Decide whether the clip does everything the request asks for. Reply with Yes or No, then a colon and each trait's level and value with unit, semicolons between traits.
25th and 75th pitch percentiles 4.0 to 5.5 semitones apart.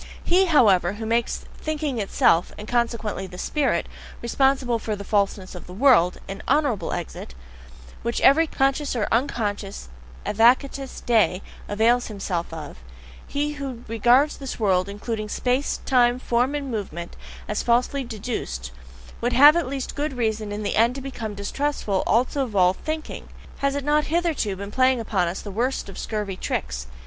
Yes: average, 5.1 semitones